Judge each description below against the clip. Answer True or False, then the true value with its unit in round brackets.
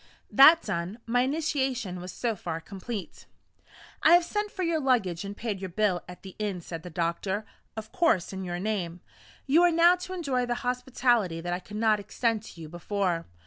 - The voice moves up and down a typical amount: False (6.6 semitones)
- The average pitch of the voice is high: True (215 Hz)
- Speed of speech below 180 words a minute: False (195 wpm)